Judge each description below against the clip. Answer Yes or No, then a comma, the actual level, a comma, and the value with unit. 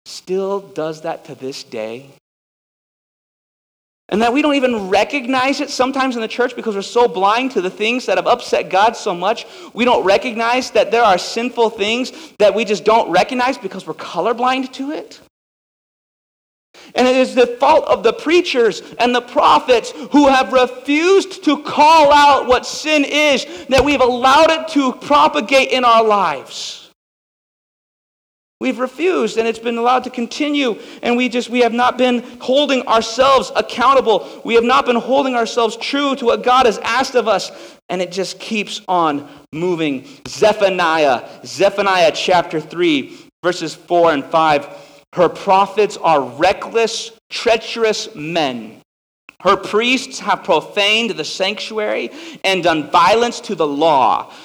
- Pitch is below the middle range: No, high, 235 Hz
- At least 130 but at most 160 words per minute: Yes, average, 155 wpm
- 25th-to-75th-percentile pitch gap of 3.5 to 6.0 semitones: Yes, average, 4.7 semitones